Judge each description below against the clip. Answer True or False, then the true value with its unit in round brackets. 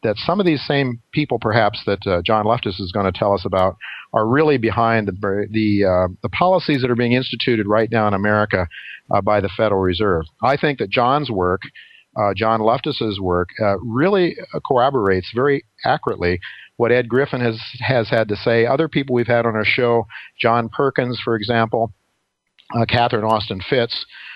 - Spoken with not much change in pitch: False (3.2 semitones)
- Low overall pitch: True (115 Hz)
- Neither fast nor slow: True (185 wpm)